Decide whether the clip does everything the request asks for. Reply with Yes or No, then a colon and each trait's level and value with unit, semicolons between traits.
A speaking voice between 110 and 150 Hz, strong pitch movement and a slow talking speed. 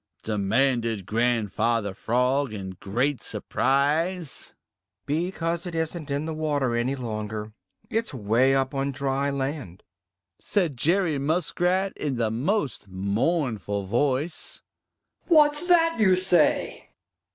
Yes: low, 135 Hz; wide, 6.4 semitones; slow, 110 wpm